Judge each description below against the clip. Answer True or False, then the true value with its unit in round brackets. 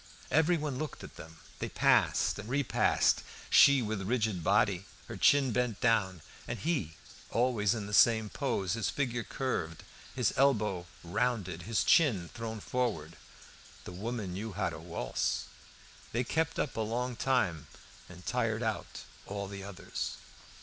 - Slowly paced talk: False (150 wpm)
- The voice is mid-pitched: False (110 Hz)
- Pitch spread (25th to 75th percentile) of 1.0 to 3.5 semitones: False (4.5 semitones)